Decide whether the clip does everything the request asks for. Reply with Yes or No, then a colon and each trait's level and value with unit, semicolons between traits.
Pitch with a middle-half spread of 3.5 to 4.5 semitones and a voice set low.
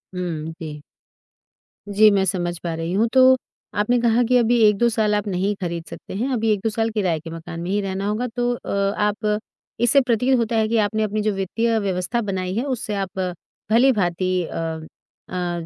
No: average, 4.1 semitones; high, 210 Hz